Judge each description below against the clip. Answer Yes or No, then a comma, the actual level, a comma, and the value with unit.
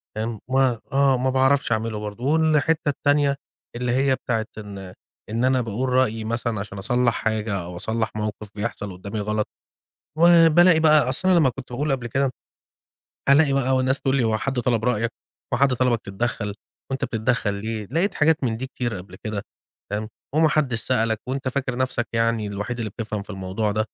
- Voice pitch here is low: Yes, low, 120 Hz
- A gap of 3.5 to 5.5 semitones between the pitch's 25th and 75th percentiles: Yes, average, 3.8 semitones